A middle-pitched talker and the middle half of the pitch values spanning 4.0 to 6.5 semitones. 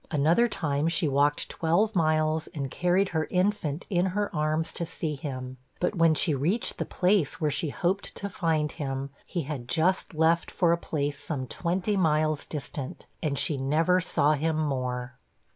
No: medium, 155 Hz; average, 3.5 semitones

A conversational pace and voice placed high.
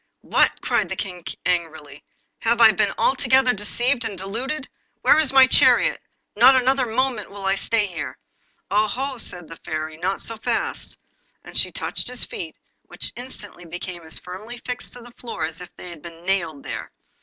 Yes: average, 180 wpm; high, 210 Hz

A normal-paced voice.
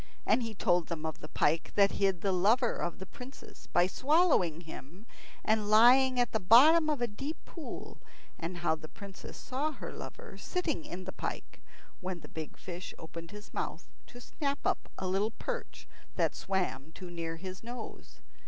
Yes: average, 180 wpm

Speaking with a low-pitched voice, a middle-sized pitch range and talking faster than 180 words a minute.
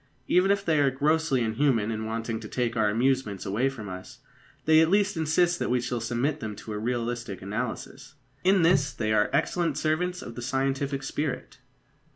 No: low, 130 Hz; wide, 5.8 semitones; average, 190 wpm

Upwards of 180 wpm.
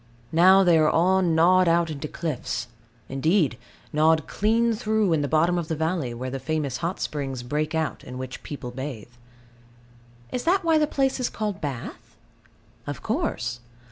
No: average, 170 wpm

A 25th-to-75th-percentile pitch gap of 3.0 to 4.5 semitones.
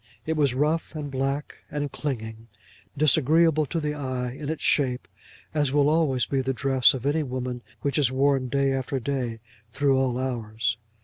No: narrow, 2.6 semitones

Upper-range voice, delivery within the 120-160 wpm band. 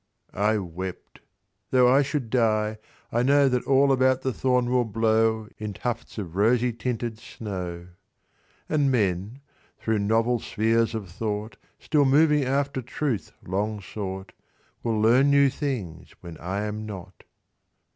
No: low, 115 Hz; average, 140 wpm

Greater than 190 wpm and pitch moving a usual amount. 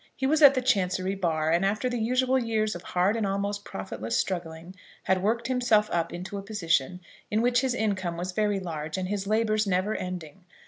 Yes: average, 200 wpm; average, 3.7 semitones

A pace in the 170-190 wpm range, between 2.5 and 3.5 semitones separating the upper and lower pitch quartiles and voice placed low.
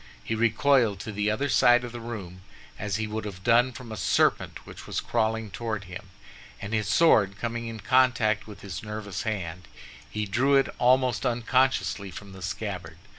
Yes: average, 180 wpm; average, 3.0 semitones; low, 110 Hz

